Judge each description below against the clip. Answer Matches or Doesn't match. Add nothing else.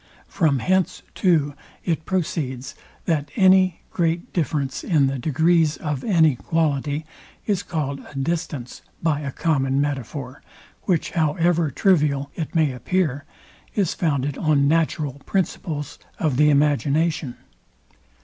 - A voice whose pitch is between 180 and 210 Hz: Doesn't match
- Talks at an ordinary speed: Doesn't match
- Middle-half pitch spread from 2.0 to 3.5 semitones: Matches